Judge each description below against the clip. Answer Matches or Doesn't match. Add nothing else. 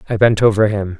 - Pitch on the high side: Doesn't match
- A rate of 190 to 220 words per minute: Doesn't match